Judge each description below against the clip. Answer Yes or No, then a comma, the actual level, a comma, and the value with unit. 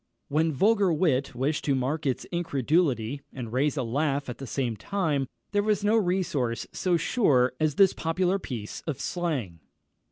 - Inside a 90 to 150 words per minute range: No, average, 165 wpm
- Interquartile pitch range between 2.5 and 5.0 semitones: No, wide, 5.6 semitones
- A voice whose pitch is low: No, medium, 150 Hz